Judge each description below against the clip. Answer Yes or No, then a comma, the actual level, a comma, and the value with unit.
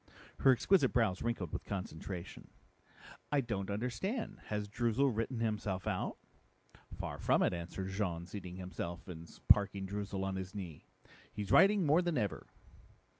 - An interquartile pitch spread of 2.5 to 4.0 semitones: No, average, 4.4 semitones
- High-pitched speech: No, low, 100 Hz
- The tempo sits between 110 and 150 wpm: Yes, average, 145 wpm